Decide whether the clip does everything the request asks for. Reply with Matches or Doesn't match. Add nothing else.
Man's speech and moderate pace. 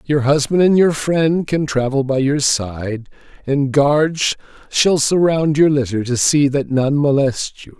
Matches